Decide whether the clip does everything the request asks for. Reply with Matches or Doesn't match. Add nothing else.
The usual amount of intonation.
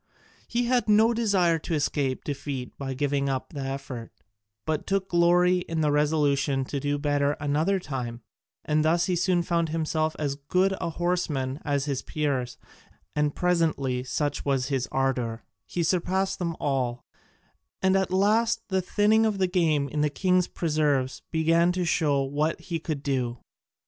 Matches